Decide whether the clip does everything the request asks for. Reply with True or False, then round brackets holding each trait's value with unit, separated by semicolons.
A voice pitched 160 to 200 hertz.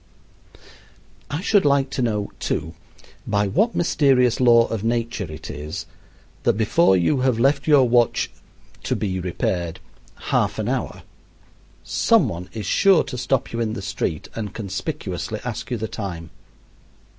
False (115 Hz)